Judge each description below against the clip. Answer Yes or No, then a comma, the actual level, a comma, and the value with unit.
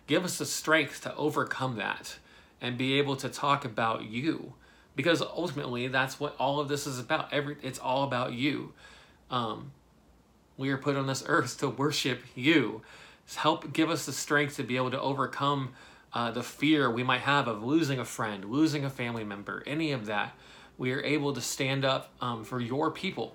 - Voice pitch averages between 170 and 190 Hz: No, low, 135 Hz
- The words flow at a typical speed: Yes, average, 195 wpm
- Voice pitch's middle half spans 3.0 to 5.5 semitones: No, narrow, 2.6 semitones